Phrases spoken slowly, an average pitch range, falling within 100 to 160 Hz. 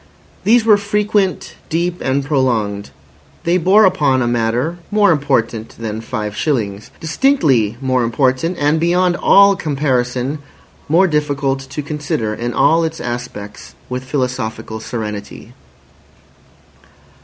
No: slow, 120 wpm; wide, 6.1 semitones; low, 135 Hz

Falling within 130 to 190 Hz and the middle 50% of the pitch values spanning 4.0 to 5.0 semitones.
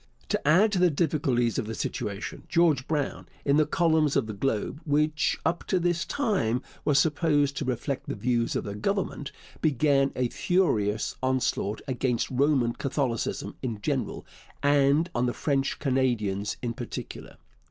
Yes: medium, 140 Hz; average, 4.3 semitones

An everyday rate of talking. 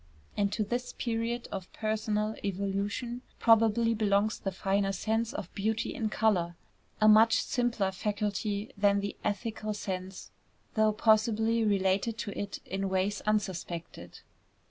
No: slow, 130 wpm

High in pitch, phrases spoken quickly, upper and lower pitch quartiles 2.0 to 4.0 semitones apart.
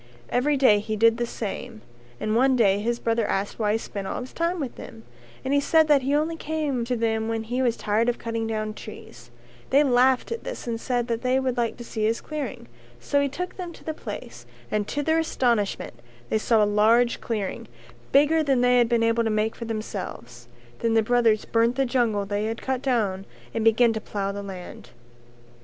Yes: high, 235 Hz; fast, 220 wpm; average, 3.4 semitones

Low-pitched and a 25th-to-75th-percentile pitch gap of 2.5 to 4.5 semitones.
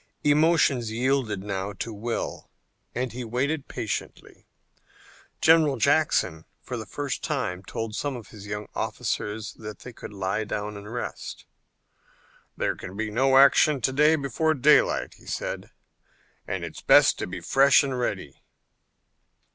No: low, 120 Hz; average, 5.0 semitones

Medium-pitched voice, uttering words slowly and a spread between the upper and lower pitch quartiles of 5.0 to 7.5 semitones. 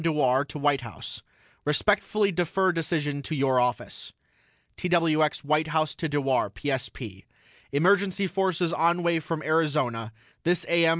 No: medium, 155 Hz; slow, 130 wpm; average, 3.4 semitones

